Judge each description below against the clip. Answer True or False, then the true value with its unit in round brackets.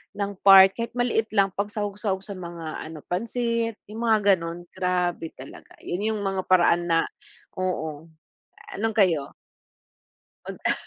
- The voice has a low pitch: False (195 Hz)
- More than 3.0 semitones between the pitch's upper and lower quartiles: True (3.5 semitones)